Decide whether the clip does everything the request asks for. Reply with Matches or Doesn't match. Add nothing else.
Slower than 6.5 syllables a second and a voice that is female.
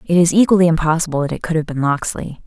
Doesn't match